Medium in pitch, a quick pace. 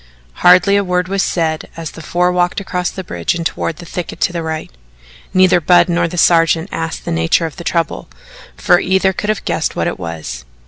Yes: medium, 175 Hz; fast, 215 wpm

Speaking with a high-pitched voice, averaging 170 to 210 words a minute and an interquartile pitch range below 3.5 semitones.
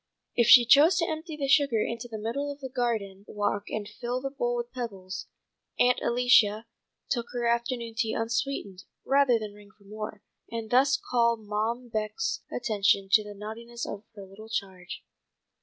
Yes: high, 230 Hz; average, 175 wpm; average, 3.0 semitones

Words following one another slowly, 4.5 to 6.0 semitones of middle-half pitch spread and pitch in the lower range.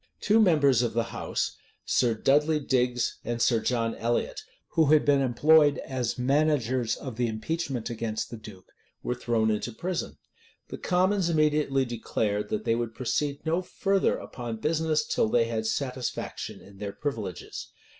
No: average, 155 wpm; average, 4.8 semitones; low, 125 Hz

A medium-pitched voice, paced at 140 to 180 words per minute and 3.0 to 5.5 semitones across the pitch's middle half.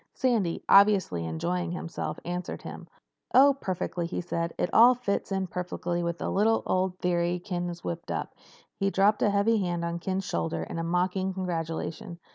No: medium, 180 Hz; average, 170 wpm; narrow, 2.4 semitones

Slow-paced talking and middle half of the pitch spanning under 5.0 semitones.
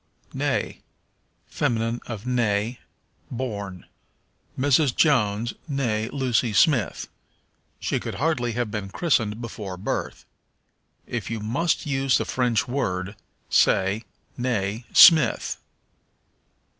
Yes: slow, 105 wpm; average, 3.8 semitones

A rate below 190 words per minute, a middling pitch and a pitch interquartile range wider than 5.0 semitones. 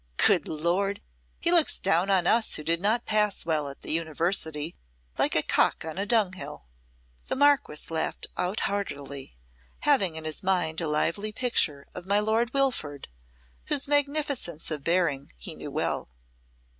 Yes: average, 155 wpm; medium, 180 Hz; wide, 5.6 semitones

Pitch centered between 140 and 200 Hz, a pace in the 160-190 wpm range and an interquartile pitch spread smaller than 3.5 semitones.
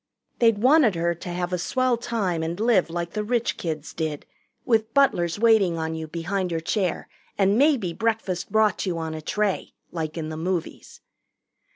No: medium, 185 Hz; average, 180 wpm; average, 5.0 semitones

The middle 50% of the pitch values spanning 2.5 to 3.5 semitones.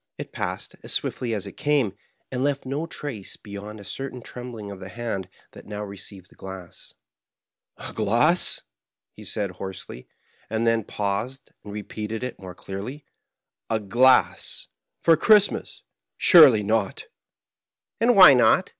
No: average, 4.8 semitones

